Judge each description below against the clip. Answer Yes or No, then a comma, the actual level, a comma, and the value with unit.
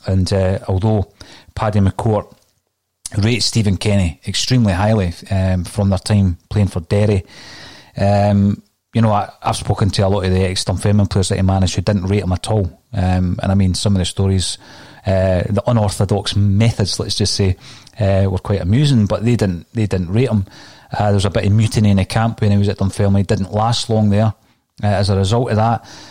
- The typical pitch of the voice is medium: No, low, 100 Hz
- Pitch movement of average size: No, narrow, 2.2 semitones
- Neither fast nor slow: No, fast, 210 wpm